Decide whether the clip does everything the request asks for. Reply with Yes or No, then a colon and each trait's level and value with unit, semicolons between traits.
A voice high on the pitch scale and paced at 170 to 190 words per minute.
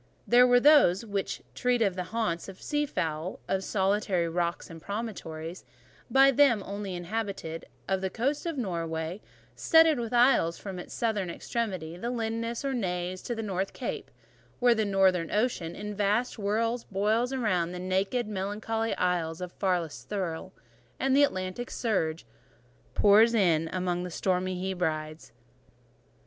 No: high, 195 Hz; average, 155 wpm